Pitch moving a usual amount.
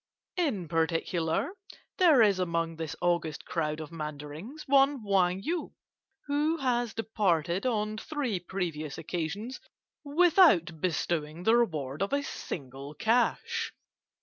No: wide, 7.8 semitones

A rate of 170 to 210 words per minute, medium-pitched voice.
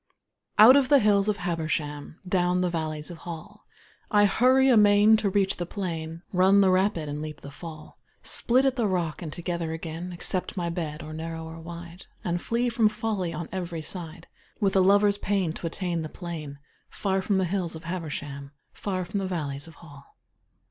Yes: average, 190 wpm; medium, 175 Hz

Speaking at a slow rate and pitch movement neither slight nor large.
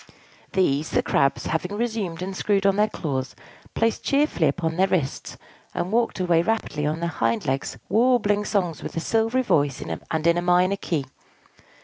No: average, 170 wpm; average, 4.9 semitones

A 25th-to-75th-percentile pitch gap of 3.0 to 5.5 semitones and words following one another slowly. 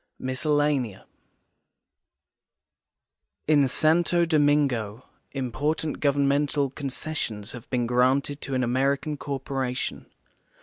No: narrow, 2.6 semitones; slow, 80 wpm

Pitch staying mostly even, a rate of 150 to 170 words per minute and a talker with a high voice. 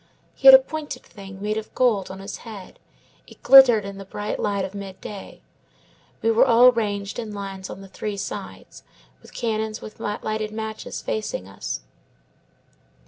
Yes: narrow, 2.3 semitones; average, 165 wpm; high, 210 Hz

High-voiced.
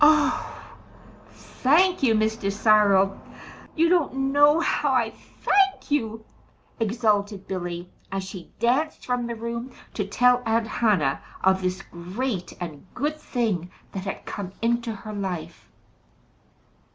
Yes: high, 225 Hz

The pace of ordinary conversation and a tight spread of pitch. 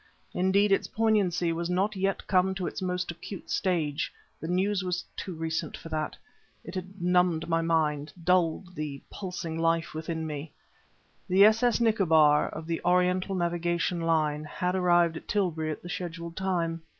Yes: average, 160 wpm; narrow, 2.3 semitones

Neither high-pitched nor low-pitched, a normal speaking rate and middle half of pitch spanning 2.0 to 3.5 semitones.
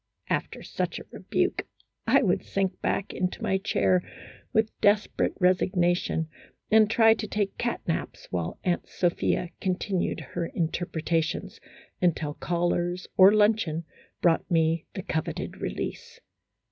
No: medium, 180 Hz; slow, 130 wpm; average, 3.2 semitones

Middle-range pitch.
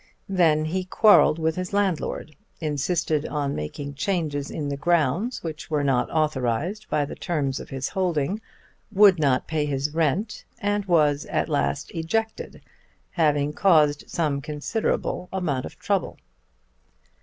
Yes: medium, 155 Hz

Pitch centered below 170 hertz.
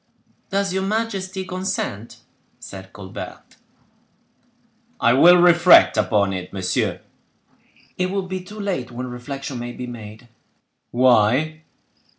Yes: low, 135 Hz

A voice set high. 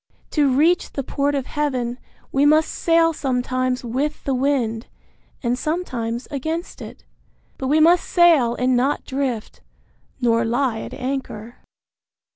Yes: very high, 265 Hz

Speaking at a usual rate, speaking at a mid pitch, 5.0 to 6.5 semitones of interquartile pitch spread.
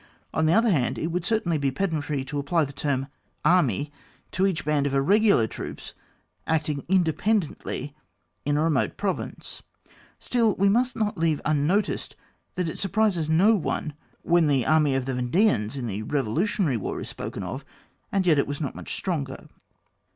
Yes: average, 175 wpm; medium, 155 Hz; average, 5.3 semitones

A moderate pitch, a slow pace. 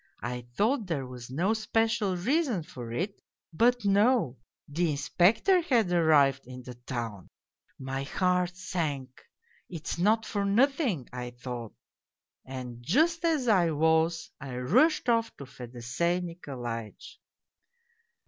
Yes: medium, 170 Hz; slow, 130 wpm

